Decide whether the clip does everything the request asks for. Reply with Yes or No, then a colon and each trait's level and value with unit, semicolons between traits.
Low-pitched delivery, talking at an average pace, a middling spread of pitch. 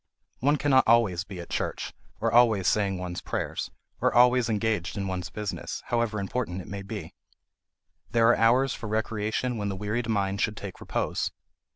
Yes: low, 105 Hz; average, 175 wpm; average, 3.3 semitones